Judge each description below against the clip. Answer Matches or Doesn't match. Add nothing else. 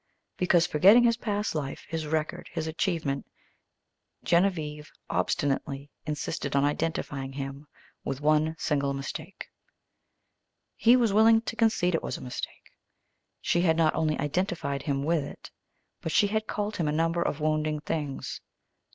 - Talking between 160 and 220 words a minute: Doesn't match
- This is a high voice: Doesn't match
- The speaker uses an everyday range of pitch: Matches